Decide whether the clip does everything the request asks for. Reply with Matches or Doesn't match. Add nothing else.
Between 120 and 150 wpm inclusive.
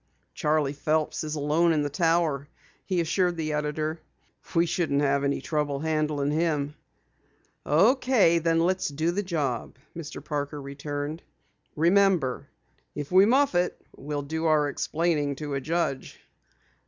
Matches